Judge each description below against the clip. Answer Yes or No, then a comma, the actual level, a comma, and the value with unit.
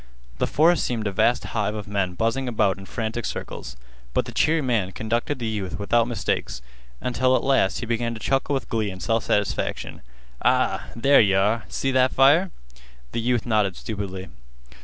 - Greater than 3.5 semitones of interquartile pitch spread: Yes, average, 4.0 semitones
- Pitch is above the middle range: No, low, 115 Hz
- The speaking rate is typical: Yes, average, 180 wpm